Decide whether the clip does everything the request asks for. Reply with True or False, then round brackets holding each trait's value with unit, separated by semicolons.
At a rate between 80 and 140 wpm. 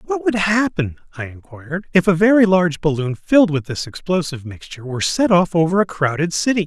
False (200 wpm)